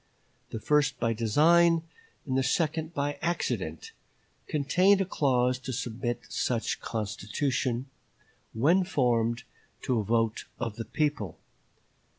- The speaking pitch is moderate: No, low, 130 Hz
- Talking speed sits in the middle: No, slow, 120 wpm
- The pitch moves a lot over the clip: No, average, 5.0 semitones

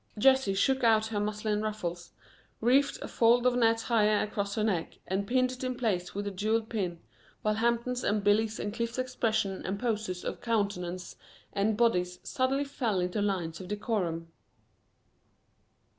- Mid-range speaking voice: No, high, 215 Hz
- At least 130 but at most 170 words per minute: Yes, average, 160 wpm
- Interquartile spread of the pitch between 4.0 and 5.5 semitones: No, average, 3.2 semitones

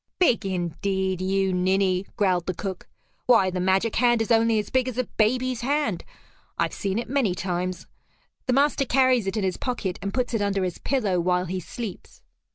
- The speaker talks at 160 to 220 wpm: Yes, average, 190 wpm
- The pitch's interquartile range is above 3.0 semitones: Yes, average, 4.7 semitones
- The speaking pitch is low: No, high, 200 Hz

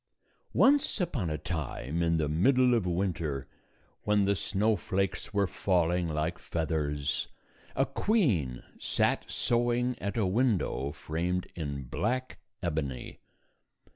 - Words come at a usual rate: No, slow, 115 wpm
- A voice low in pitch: Yes, very low, 90 Hz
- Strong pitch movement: Yes, wide, 7.0 semitones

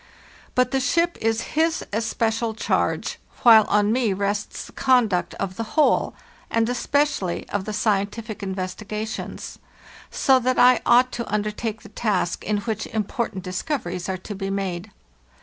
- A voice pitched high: Yes, high, 215 Hz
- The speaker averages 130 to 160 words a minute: Yes, average, 150 wpm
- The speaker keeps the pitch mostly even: No, average, 3.5 semitones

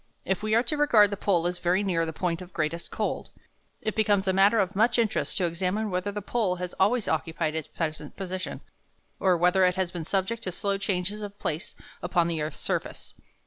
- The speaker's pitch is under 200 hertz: Yes, medium, 185 Hz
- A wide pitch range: No, average, 2.9 semitones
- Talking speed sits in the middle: No, fast, 215 wpm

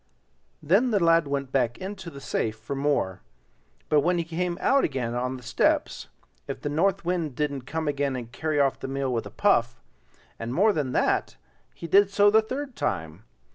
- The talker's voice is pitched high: No, medium, 145 Hz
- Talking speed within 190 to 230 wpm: Yes, average, 195 wpm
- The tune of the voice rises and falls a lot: Yes, wide, 5.9 semitones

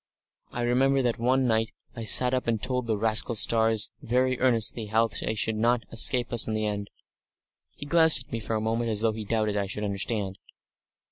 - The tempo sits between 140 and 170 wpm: No, fast, 205 wpm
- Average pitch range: No, narrow, 2.3 semitones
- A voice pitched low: Yes, low, 115 Hz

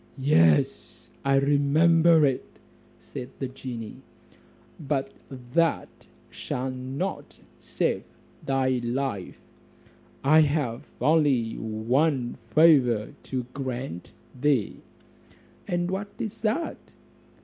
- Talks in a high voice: No, low, 135 Hz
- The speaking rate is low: Yes, slow, 90 wpm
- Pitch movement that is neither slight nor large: Yes, average, 4.1 semitones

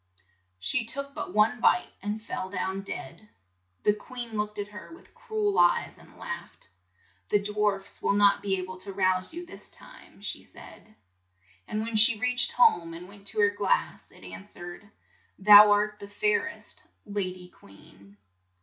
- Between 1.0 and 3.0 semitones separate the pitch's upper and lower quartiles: Yes, average, 2.7 semitones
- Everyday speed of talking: Yes, average, 180 wpm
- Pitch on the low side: No, high, 205 Hz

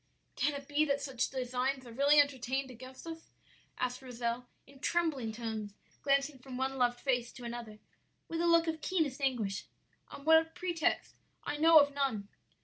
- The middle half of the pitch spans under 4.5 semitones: Yes, average, 3.2 semitones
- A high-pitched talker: Yes, very high, 270 Hz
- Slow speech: No, average, 170 wpm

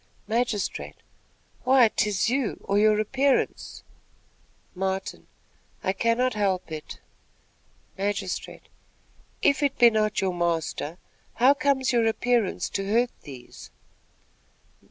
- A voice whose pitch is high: Yes, high, 215 Hz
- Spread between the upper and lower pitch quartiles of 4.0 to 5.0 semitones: Yes, average, 4.4 semitones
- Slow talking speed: Yes, slow, 105 wpm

